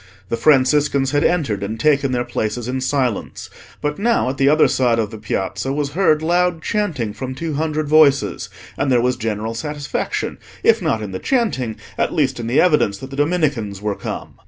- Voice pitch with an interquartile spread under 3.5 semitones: No, average, 5.0 semitones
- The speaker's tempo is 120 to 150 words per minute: No, average, 195 wpm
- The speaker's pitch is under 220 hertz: Yes, low, 135 Hz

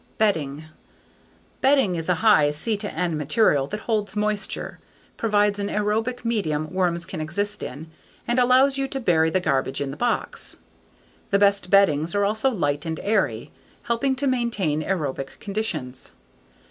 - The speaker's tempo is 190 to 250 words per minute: No, average, 145 wpm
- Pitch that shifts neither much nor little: No, wide, 6.0 semitones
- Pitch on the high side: Yes, high, 200 Hz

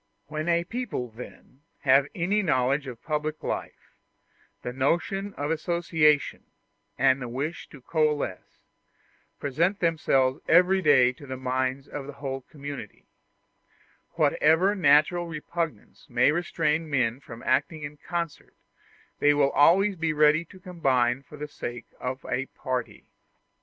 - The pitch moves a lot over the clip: No, average, 4.1 semitones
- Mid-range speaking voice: Yes, medium, 145 Hz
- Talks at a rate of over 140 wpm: No, slow, 135 wpm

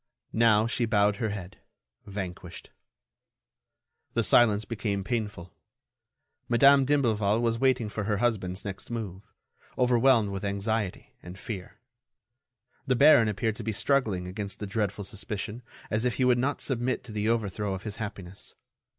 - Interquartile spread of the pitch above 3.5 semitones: No, average, 3.0 semitones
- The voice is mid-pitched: No, low, 110 Hz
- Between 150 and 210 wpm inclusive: No, average, 140 wpm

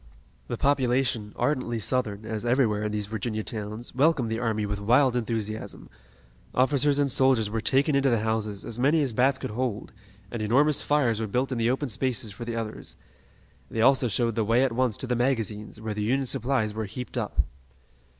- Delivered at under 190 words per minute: No, average, 195 wpm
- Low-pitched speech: Yes, low, 120 Hz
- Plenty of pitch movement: No, average, 3.3 semitones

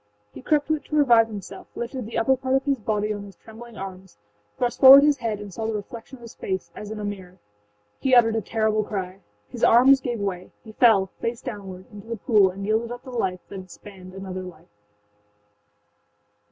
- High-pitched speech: Yes, high, 220 Hz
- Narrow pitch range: No, average, 3.7 semitones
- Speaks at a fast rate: Yes, fast, 215 wpm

